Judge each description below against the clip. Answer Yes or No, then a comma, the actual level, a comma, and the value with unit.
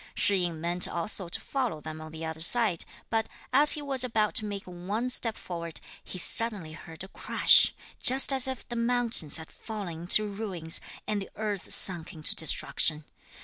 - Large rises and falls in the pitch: Yes, wide, 5.7 semitones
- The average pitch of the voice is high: Yes, high, 195 Hz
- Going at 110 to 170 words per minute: No, average, 185 wpm